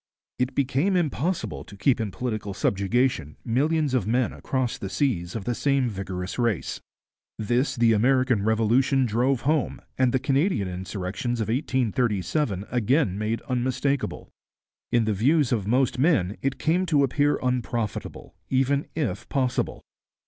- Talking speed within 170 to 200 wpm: No, average, 140 wpm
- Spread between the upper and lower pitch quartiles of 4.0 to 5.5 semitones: Yes, average, 4.3 semitones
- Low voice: Yes, low, 125 Hz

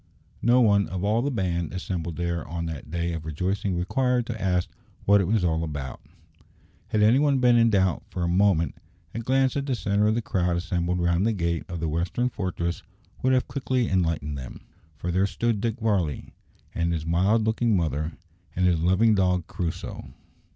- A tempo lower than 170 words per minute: No, average, 195 wpm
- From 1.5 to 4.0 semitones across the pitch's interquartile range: No, average, 4.7 semitones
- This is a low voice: Yes, very low, 90 Hz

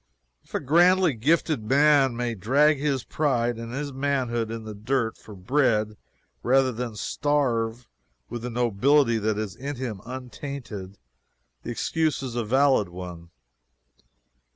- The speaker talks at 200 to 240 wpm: No, average, 140 wpm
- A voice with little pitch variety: No, average, 4.0 semitones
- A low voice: Yes, low, 125 Hz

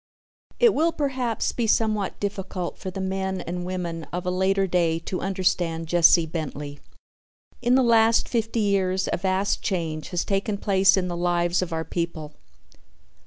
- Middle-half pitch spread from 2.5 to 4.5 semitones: Yes, average, 2.8 semitones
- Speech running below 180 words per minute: Yes, average, 165 wpm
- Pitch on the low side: No, medium, 185 Hz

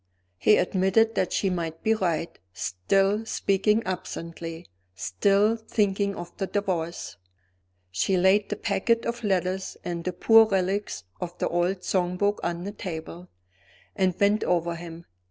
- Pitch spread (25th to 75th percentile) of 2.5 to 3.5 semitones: Yes, average, 2.8 semitones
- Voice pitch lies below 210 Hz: Yes, high, 190 Hz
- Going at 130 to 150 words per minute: Yes, average, 145 wpm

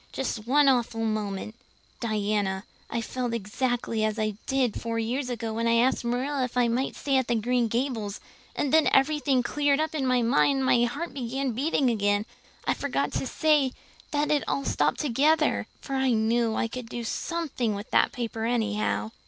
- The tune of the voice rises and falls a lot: No, average, 3.3 semitones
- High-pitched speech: Yes, high, 245 Hz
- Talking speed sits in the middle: Yes, average, 185 wpm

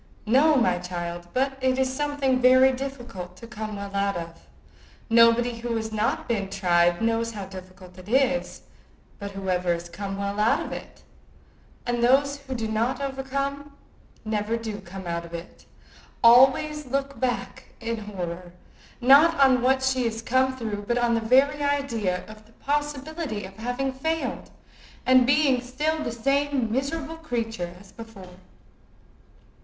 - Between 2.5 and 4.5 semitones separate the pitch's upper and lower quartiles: No, average, 5.0 semitones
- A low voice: No, high, 235 Hz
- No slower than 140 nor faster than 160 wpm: Yes, average, 155 wpm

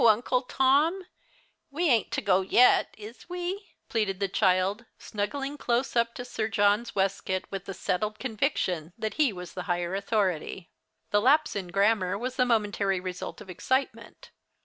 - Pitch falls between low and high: No, high, 215 Hz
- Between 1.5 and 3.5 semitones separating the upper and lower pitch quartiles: No, average, 4.7 semitones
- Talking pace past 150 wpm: Yes, average, 160 wpm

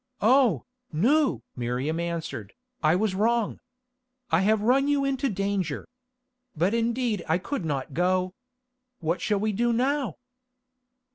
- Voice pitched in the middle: No, high, 200 Hz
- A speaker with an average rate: No, slow, 130 wpm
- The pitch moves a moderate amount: No, wide, 6.3 semitones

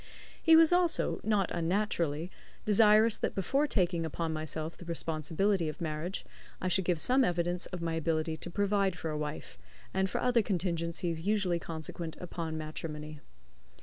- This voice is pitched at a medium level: Yes, medium, 170 Hz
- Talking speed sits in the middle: Yes, average, 155 wpm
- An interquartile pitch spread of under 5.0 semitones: Yes, average, 3.8 semitones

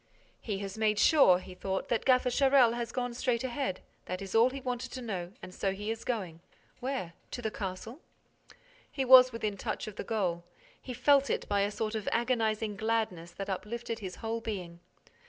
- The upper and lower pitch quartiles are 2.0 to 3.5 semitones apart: No, average, 4.0 semitones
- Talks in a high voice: Yes, high, 220 Hz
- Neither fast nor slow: Yes, average, 190 wpm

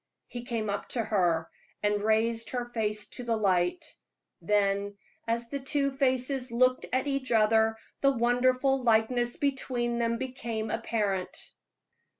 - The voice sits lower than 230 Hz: No, high, 235 Hz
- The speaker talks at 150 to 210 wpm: No, average, 140 wpm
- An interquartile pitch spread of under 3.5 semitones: Yes, average, 3.0 semitones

